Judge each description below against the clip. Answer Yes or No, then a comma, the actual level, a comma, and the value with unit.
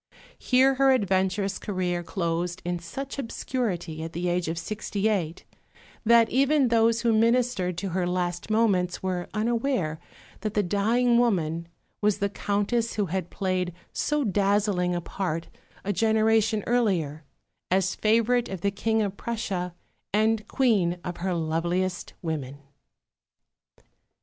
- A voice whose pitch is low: No, high, 200 Hz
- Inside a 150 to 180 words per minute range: No, slow, 135 wpm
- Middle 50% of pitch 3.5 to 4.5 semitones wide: Yes, average, 4.2 semitones